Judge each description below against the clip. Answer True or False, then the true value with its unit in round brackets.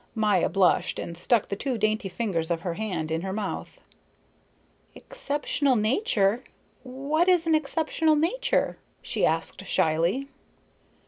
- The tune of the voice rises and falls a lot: True (7.6 semitones)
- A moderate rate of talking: False (130 wpm)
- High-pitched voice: True (220 Hz)